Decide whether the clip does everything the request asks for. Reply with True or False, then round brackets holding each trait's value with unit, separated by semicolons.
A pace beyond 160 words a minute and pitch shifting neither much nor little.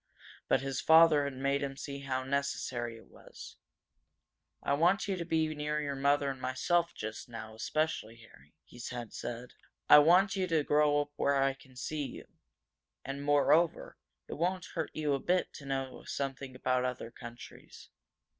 True (175 wpm; 3.1 semitones)